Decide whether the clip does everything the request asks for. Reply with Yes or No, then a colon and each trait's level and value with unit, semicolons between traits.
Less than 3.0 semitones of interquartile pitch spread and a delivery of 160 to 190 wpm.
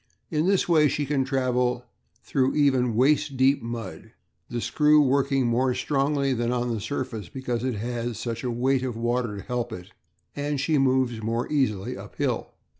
Yes: narrow, 2.6 semitones; average, 175 wpm